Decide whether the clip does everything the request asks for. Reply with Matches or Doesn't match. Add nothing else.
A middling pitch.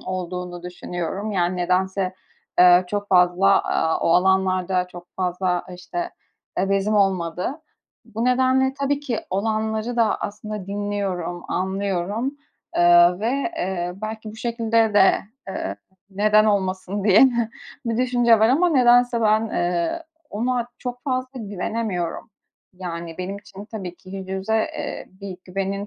Doesn't match